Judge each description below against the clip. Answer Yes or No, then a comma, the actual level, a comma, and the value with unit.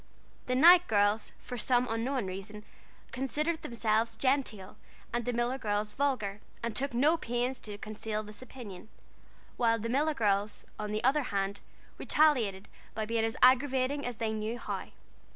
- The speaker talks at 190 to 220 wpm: No, average, 155 wpm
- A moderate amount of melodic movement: Yes, average, 3.6 semitones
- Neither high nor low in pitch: No, high, 230 Hz